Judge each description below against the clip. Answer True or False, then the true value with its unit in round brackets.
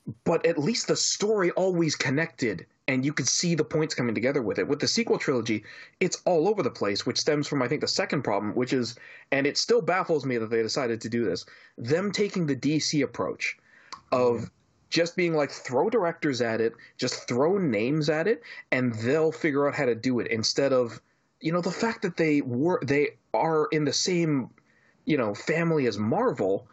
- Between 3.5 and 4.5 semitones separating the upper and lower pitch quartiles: False (4.9 semitones)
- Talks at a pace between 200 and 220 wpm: True (205 wpm)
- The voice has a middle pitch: True (145 Hz)